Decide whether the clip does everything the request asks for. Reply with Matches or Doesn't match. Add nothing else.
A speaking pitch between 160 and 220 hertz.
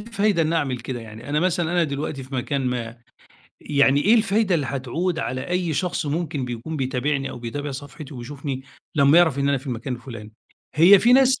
Doesn't match